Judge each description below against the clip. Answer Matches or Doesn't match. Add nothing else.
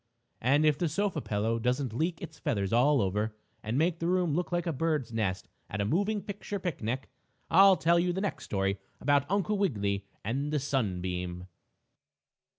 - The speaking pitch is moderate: Matches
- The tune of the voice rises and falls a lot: Matches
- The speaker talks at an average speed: Matches